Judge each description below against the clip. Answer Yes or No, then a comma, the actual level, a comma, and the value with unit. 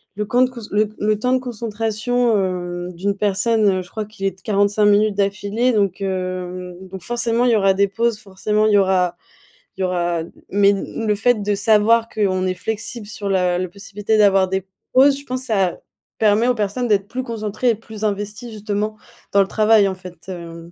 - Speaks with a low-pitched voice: No, high, 205 Hz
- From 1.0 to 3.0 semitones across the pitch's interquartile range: Yes, narrow, 2.6 semitones